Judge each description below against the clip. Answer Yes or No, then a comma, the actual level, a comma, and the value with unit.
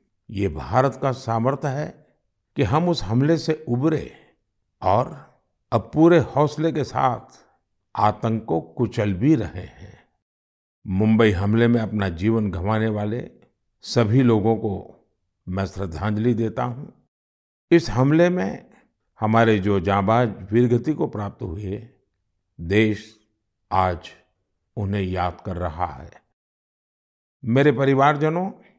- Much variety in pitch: No, average, 5.0 semitones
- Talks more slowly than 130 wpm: Yes, average, 115 wpm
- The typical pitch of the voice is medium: No, low, 110 Hz